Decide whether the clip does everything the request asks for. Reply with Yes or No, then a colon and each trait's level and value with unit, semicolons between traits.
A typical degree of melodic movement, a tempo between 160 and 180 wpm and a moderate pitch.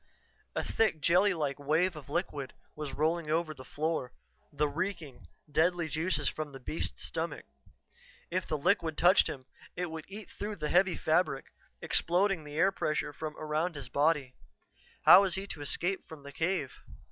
Yes: average, 3.5 semitones; average, 170 wpm; medium, 160 Hz